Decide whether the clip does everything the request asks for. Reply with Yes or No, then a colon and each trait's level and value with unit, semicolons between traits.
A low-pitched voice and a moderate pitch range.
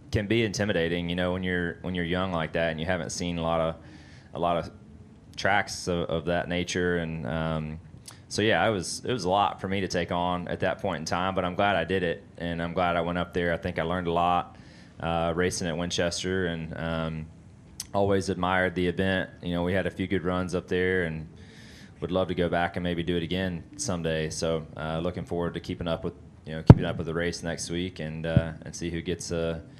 No: very low, 85 Hz; narrow, 1.8 semitones